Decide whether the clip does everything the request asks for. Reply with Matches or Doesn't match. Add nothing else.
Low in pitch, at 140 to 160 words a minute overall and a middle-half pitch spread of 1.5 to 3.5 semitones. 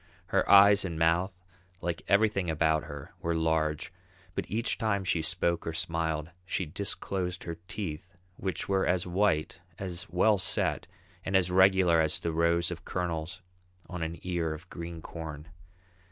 Matches